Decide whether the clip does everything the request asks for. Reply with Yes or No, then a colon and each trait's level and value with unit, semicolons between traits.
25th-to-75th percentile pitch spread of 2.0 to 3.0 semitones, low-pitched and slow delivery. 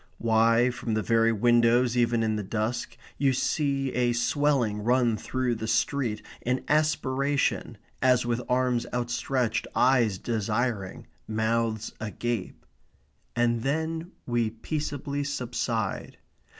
Yes: narrow, 2.5 semitones; low, 120 Hz; slow, 115 wpm